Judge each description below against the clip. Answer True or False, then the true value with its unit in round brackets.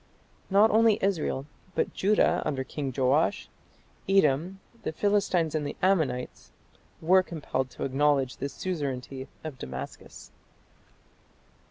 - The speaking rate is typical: False (115 wpm)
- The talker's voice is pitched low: False (155 Hz)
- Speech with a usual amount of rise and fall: False (6.0 semitones)